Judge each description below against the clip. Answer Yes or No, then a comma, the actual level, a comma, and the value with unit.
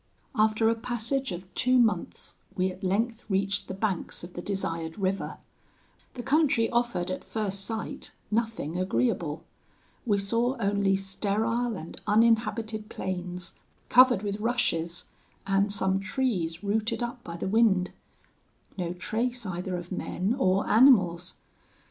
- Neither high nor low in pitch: No, high, 200 Hz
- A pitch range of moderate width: Yes, average, 3.7 semitones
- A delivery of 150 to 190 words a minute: No, slow, 135 wpm